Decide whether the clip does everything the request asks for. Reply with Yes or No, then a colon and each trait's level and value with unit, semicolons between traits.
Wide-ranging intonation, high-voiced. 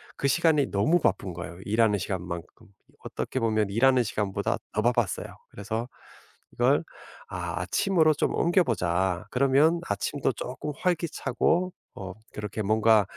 No: wide, 6.6 semitones; low, 110 Hz